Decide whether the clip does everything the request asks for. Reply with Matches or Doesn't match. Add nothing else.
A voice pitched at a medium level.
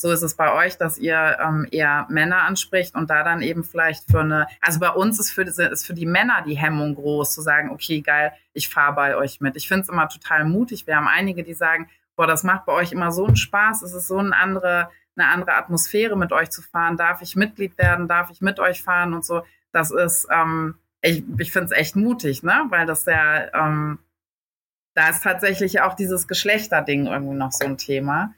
Matches